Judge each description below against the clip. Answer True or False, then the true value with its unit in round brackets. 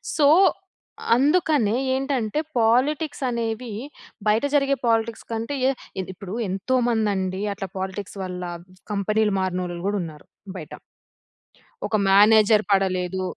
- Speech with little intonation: False (3.8 semitones)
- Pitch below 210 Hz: False (215 Hz)